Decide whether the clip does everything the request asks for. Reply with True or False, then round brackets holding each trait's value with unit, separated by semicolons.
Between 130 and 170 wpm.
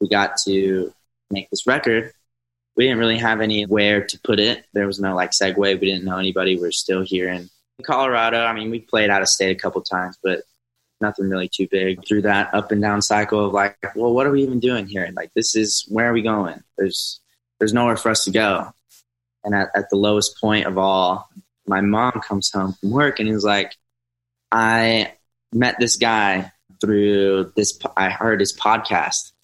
False (205 wpm)